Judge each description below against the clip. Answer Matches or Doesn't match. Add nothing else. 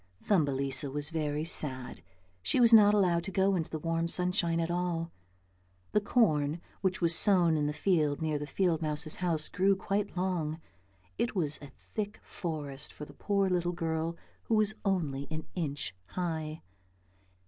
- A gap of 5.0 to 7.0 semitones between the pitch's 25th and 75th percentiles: Doesn't match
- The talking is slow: Doesn't match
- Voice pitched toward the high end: Doesn't match